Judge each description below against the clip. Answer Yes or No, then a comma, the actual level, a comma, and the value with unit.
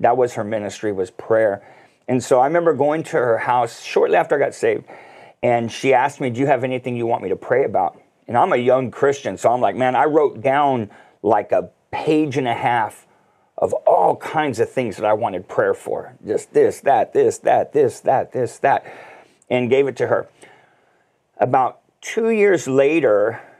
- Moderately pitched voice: Yes, medium, 150 Hz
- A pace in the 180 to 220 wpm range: Yes, average, 200 wpm